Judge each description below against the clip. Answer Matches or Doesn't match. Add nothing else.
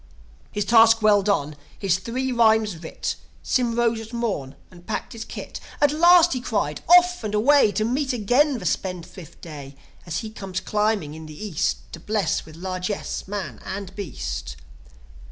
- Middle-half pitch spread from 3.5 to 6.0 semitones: Matches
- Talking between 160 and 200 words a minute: Matches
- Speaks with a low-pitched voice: Doesn't match